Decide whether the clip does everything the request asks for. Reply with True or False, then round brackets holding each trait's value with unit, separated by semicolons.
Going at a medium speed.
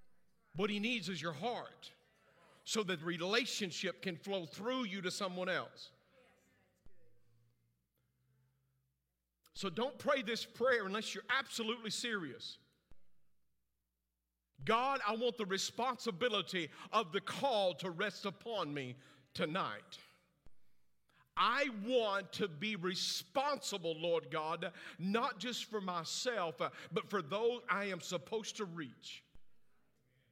False (115 wpm)